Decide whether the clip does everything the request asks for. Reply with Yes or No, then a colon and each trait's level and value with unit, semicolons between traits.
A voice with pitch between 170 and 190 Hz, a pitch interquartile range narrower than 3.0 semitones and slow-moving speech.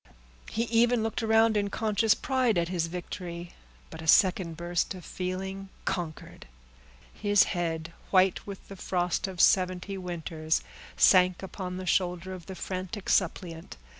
No: medium, 185 Hz; narrow, 2.5 semitones; average, 145 wpm